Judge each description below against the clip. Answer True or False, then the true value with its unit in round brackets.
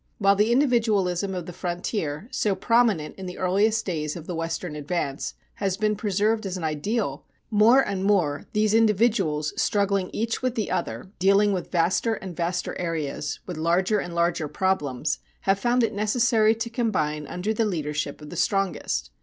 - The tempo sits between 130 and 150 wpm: False (170 wpm)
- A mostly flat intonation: False (4.3 semitones)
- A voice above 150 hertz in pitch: True (190 Hz)